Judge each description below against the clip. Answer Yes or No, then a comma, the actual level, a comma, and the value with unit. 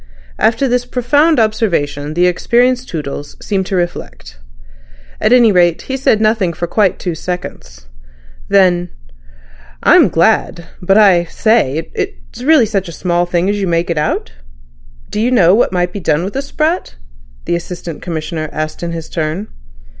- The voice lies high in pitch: No, medium, 180 Hz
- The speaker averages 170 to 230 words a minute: No, average, 160 wpm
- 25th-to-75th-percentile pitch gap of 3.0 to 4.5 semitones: No, average, 4.9 semitones